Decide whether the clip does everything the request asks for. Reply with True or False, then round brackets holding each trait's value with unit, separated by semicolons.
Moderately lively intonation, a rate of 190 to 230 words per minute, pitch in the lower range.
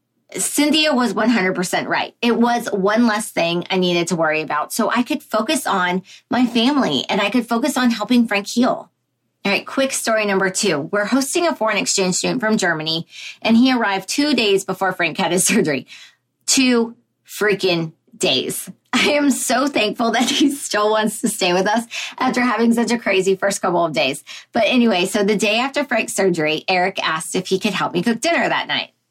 False (4.7 semitones; 200 wpm; 215 Hz)